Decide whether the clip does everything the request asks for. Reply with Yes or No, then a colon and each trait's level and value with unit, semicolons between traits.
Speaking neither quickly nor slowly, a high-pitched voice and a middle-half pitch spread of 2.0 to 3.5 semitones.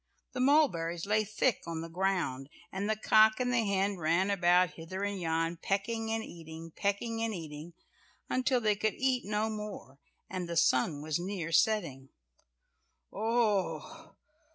No: average, 150 wpm; high, 195 Hz; average, 4.7 semitones